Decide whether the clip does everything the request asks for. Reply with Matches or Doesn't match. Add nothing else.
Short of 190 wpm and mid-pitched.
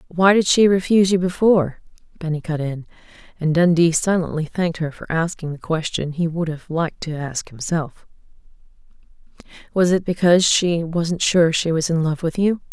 Matches